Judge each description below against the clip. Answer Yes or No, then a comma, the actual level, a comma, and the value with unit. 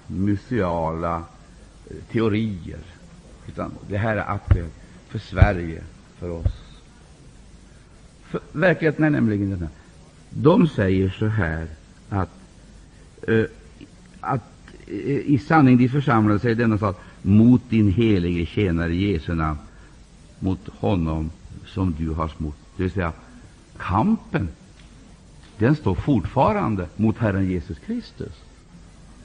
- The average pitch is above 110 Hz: No, very low, 95 Hz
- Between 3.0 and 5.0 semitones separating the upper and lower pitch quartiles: Yes, average, 4.5 semitones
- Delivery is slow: Yes, slow, 105 wpm